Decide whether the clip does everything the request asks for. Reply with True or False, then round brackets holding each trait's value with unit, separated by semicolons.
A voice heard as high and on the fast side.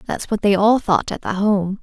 True (200 Hz; 265 wpm)